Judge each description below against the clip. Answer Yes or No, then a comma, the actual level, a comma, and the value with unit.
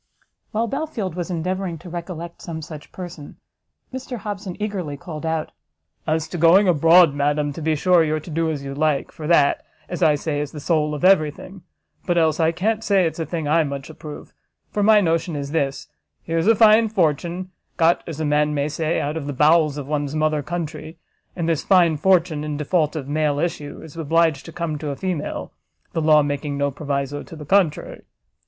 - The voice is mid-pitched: Yes, medium, 160 Hz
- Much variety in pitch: No, average, 2.9 semitones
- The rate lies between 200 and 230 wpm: Yes, fast, 205 wpm